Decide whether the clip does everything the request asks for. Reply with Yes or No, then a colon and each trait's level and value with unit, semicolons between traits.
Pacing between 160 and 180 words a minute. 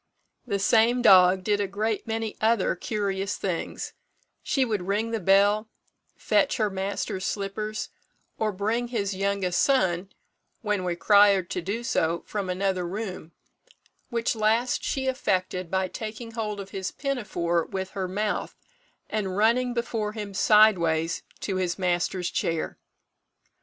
No: slow, 135 wpm